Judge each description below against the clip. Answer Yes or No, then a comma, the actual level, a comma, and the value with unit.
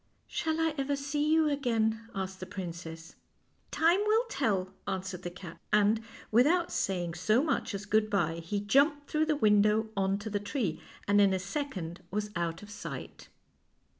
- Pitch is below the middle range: No, high, 210 Hz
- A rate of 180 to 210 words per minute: Yes, average, 190 wpm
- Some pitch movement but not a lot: No, wide, 7.0 semitones